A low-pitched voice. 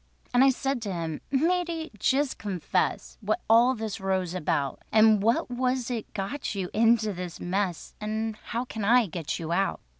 No: high, 215 Hz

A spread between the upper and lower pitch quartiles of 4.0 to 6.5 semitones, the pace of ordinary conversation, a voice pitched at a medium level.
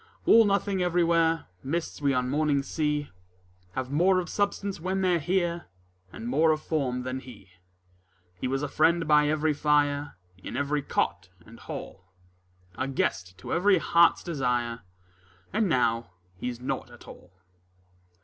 Yes: average, 5.0 semitones; average, 150 wpm; medium, 150 Hz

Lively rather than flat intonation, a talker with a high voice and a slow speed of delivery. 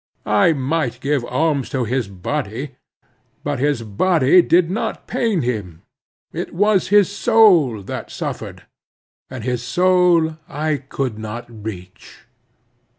No: wide, 6.5 semitones; medium, 140 Hz; slow, 125 wpm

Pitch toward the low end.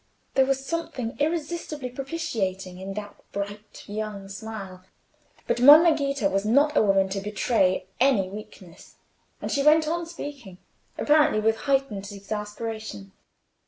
No: high, 220 Hz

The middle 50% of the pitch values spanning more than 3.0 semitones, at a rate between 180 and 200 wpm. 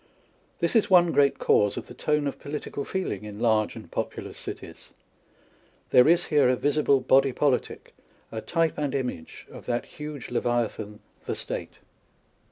No: average, 4.1 semitones; average, 165 wpm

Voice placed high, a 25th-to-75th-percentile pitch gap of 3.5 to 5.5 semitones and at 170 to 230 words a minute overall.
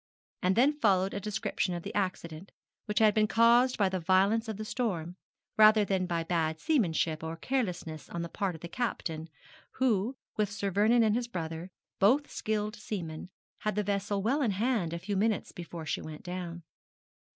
Yes: high, 200 Hz; average, 4.2 semitones; average, 185 wpm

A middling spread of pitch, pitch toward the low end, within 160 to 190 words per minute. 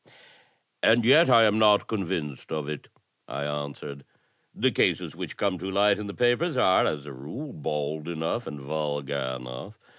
No: wide, 6.7 semitones; very low, 80 Hz; average, 170 wpm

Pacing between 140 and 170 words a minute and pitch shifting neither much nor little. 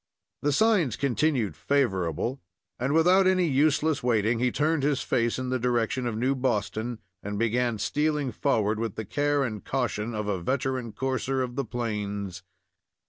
Yes: average, 160 wpm; average, 4.3 semitones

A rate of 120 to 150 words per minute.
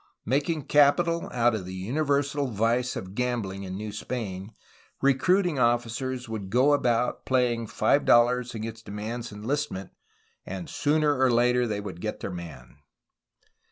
Yes: average, 145 wpm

